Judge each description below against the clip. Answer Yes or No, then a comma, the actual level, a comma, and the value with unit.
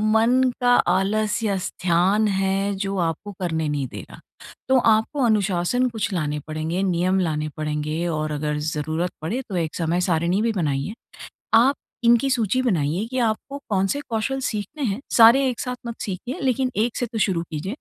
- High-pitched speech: Yes, high, 195 Hz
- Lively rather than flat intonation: Yes, wide, 5.8 semitones